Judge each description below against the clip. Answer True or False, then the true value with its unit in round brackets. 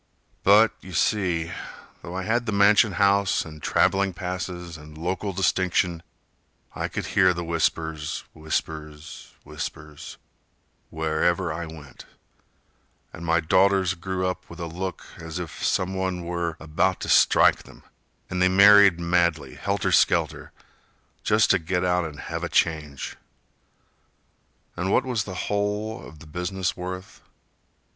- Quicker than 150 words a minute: False (140 wpm)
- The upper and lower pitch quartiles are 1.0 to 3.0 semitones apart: True (2.7 semitones)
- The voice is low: True (90 Hz)